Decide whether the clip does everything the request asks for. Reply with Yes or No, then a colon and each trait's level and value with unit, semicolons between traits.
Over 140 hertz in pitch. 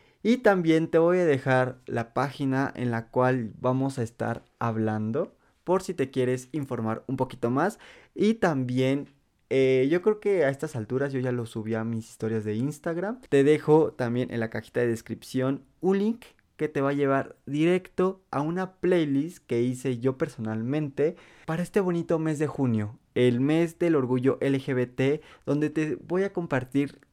No: low, 135 Hz